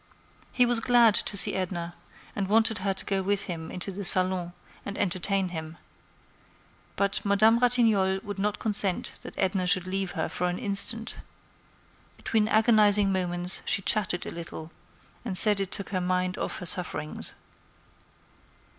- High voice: Yes, high, 195 Hz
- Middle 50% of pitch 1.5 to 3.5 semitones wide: Yes, narrow, 2.5 semitones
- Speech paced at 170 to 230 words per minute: No, average, 155 wpm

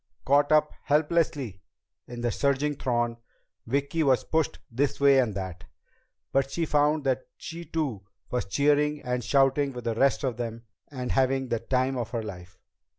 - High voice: No, low, 135 Hz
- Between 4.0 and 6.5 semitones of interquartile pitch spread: No, average, 3.4 semitones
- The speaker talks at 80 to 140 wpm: No, average, 165 wpm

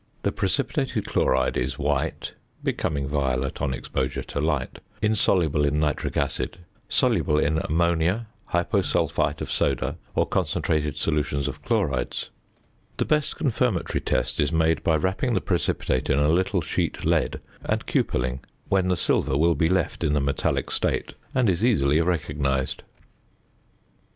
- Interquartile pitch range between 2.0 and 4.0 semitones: Yes, average, 3.7 semitones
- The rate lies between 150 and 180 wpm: No, average, 140 wpm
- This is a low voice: Yes, very low, 75 Hz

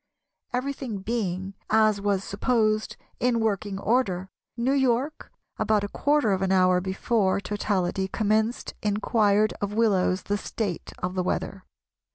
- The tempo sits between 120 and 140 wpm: Yes, slow, 135 wpm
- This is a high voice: Yes, high, 205 Hz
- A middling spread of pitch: Yes, average, 3.1 semitones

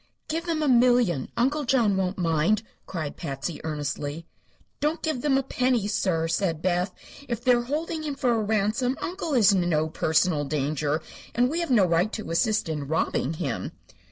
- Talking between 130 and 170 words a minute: No, average, 185 wpm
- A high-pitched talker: Yes, high, 205 Hz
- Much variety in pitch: Yes, wide, 7.8 semitones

